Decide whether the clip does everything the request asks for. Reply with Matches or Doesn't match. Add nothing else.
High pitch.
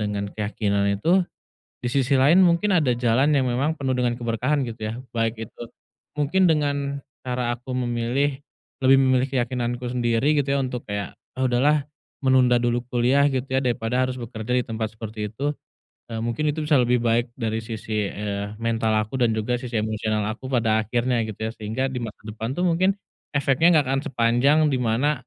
Doesn't match